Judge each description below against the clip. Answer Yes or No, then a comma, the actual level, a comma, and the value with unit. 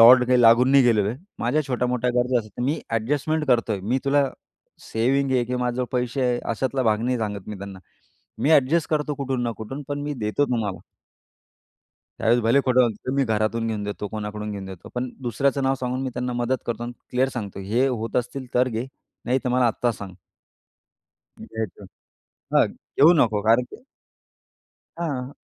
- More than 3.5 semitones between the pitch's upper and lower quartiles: No, average, 2.9 semitones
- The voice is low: Yes, low, 125 Hz